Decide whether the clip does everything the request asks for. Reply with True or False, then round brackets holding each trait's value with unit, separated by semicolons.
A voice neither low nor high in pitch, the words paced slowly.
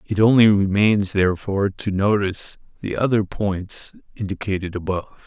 False (100 Hz; 125 wpm)